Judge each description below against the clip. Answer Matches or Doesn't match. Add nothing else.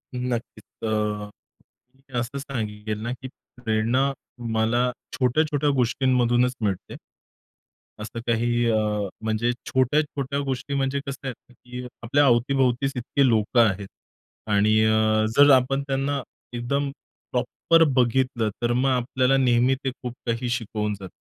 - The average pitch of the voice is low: Matches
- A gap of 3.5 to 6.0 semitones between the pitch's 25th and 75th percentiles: Doesn't match